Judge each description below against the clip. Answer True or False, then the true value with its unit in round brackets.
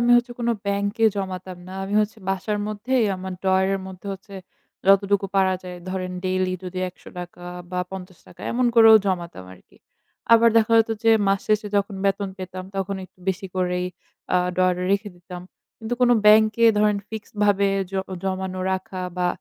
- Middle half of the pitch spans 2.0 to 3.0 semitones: True (2.4 semitones)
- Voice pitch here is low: False (195 Hz)